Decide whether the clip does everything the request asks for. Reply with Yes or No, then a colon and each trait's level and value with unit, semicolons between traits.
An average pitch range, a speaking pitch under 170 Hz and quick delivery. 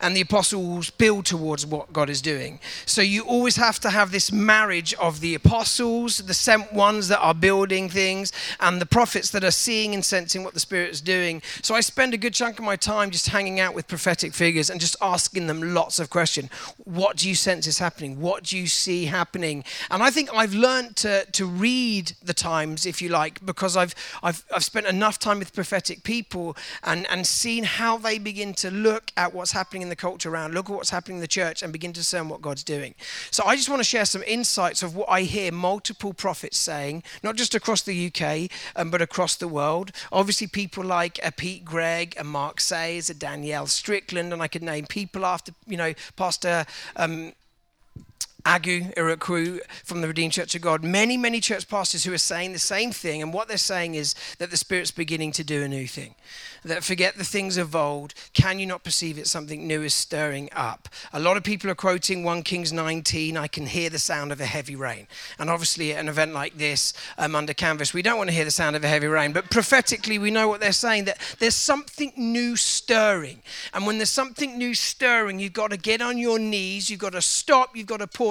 No: average, 4.0 semitones; medium, 180 Hz; fast, 225 wpm